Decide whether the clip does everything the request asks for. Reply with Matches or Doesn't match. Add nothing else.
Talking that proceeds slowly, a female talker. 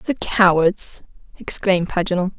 Matches